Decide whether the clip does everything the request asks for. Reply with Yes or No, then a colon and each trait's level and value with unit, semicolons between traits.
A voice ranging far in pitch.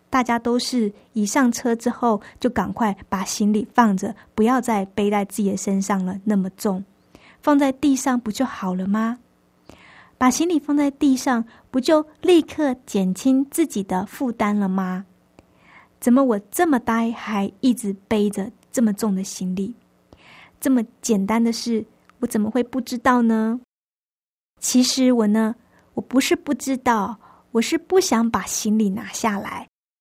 No: average, 3.8 semitones